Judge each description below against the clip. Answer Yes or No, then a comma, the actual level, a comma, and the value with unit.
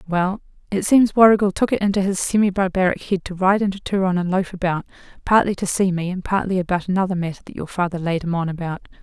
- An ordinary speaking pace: No, fast, 225 wpm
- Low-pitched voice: No, medium, 185 Hz